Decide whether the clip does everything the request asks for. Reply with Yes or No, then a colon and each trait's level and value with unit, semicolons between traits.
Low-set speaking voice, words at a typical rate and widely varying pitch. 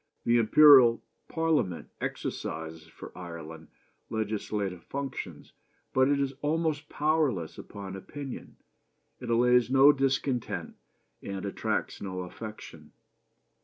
No: low, 115 Hz; slow, 100 wpm; wide, 6.7 semitones